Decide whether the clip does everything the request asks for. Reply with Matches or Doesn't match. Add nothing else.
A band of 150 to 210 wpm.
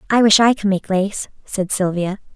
Matches